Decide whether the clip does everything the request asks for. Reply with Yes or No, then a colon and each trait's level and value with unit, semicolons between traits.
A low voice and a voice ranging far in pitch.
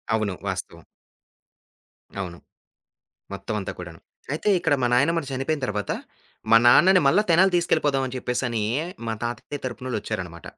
Yes: low, 125 Hz; wide, 6.9 semitones